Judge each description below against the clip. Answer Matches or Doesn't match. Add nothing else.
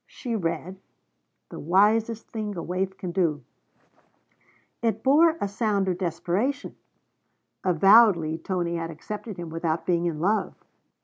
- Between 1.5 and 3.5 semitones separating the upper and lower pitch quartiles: Doesn't match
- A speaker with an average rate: Doesn't match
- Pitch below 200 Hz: Matches